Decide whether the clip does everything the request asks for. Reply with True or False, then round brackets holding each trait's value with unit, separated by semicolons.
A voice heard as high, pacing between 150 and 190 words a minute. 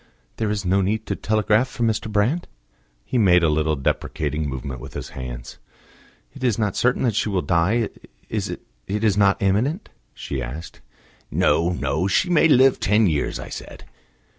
False (100 Hz; 170 wpm)